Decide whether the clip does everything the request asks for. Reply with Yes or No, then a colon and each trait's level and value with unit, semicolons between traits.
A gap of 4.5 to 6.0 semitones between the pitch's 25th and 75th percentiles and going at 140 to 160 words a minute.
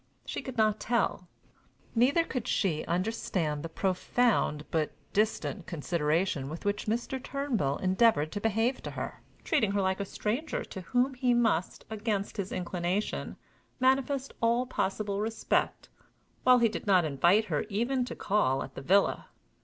Yes: average, 5.1 semitones; average, 155 wpm